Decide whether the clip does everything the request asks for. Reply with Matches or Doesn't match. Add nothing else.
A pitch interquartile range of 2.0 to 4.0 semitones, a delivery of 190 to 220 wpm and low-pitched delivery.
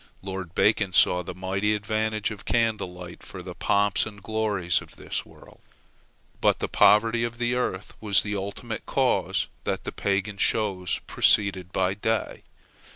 Doesn't match